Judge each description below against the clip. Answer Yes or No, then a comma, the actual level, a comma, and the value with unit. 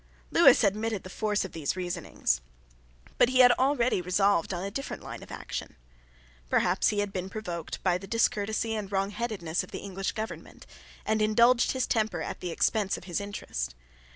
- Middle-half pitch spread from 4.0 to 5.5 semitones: No, average, 3.2 semitones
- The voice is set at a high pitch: Yes, high, 205 Hz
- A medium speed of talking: Yes, average, 180 wpm